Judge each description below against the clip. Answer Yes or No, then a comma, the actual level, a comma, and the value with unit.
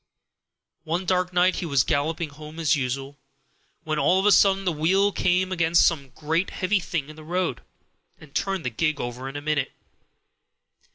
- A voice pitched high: No, medium, 160 Hz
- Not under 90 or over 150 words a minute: No, average, 180 wpm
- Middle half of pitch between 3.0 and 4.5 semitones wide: Yes, average, 4.0 semitones